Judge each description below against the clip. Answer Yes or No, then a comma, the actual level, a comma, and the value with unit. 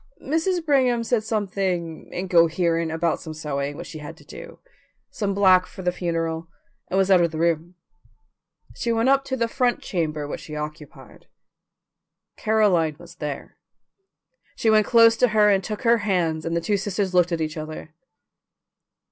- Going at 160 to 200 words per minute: Yes, average, 170 wpm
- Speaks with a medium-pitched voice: Yes, medium, 180 Hz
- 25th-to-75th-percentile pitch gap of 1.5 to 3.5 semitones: No, average, 5.1 semitones